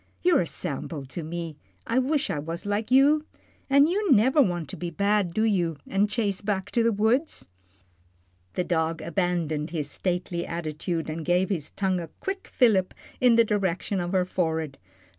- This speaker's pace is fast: No, average, 180 wpm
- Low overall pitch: No, medium, 185 Hz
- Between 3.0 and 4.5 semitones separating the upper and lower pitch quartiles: No, average, 5.1 semitones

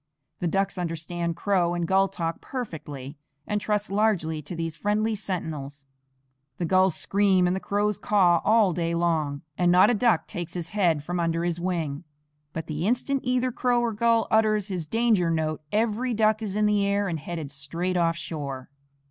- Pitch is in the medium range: Yes, medium, 180 Hz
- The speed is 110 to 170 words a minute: No, average, 180 wpm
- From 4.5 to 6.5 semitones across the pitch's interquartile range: No, average, 4.1 semitones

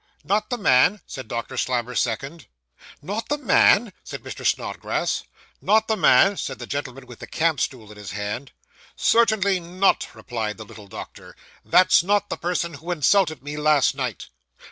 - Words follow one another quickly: No, average, 165 wpm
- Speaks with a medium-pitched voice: Yes, medium, 150 Hz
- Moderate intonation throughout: No, wide, 7.8 semitones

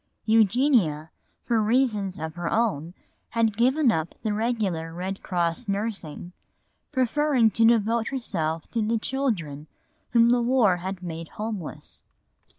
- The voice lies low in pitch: No, high, 215 Hz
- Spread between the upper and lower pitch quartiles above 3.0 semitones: Yes, average, 5.2 semitones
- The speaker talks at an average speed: No, slow, 130 wpm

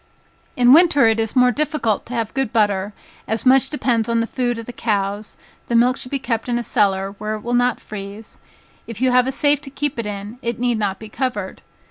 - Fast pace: Yes, fast, 230 wpm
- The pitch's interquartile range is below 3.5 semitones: Yes, average, 3.1 semitones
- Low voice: No, high, 235 Hz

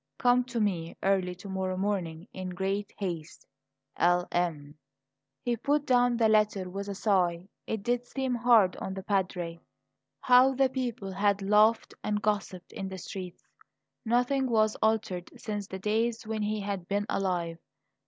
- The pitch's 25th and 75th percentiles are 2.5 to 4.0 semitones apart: Yes, average, 3.6 semitones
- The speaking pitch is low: No, high, 200 Hz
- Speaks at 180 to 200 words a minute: No, average, 160 wpm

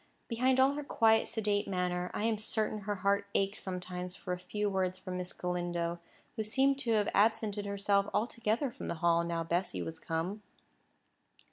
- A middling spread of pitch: Yes, average, 3.4 semitones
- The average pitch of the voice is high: Yes, high, 200 Hz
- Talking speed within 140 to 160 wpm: No, average, 175 wpm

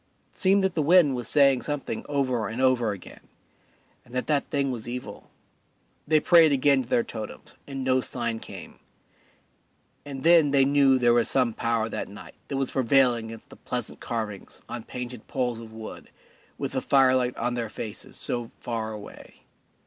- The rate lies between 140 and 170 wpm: No, average, 180 wpm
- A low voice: Yes, low, 125 Hz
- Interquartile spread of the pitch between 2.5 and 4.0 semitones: Yes, average, 3.1 semitones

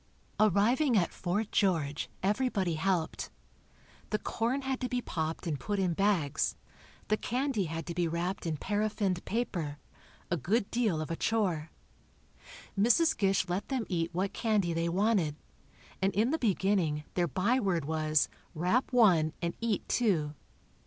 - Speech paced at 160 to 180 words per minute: No, average, 150 wpm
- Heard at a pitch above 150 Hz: Yes, high, 190 Hz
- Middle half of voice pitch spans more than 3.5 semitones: Yes, average, 4.9 semitones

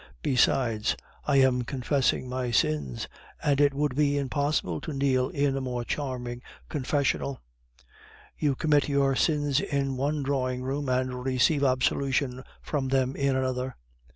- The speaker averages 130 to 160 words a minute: Yes, average, 140 wpm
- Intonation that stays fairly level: Yes, narrow, 1.9 semitones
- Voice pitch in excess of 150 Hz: No, low, 135 Hz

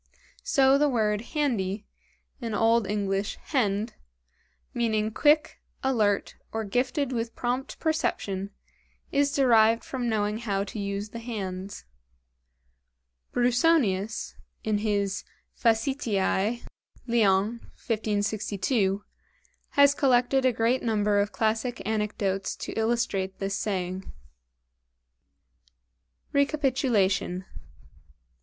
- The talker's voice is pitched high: Yes, high, 220 Hz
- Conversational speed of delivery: No, slow, 90 wpm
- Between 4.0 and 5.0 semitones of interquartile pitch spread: No, average, 3.5 semitones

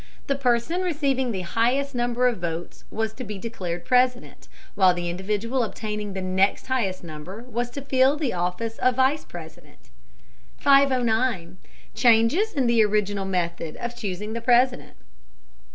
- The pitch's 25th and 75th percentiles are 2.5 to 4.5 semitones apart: No, average, 5.1 semitones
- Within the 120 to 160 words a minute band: Yes, average, 150 wpm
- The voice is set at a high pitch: Yes, high, 230 Hz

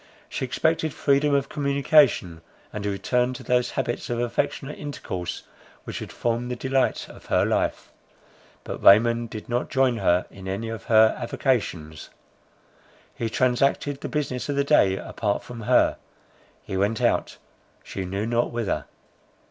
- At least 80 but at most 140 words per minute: No, average, 155 wpm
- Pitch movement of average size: Yes, average, 4.2 semitones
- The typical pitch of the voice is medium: No, low, 120 Hz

